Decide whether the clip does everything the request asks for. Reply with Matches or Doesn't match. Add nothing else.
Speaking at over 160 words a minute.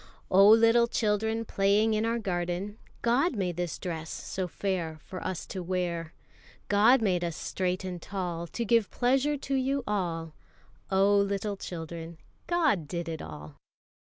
Doesn't match